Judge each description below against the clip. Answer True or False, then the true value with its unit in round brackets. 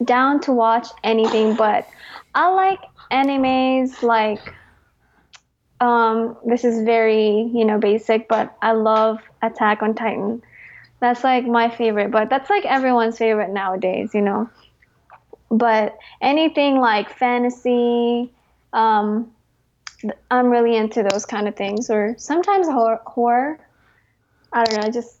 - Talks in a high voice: True (230 Hz)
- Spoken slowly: True (130 wpm)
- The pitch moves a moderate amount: False (2.2 semitones)